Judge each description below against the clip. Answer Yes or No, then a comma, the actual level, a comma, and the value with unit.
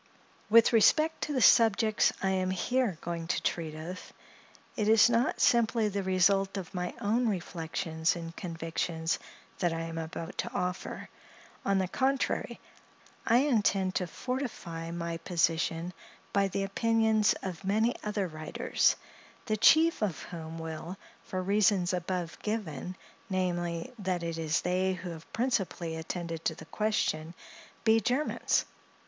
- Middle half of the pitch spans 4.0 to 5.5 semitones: Yes, average, 4.5 semitones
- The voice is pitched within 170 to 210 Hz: Yes, medium, 185 Hz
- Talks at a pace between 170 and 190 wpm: No, average, 145 wpm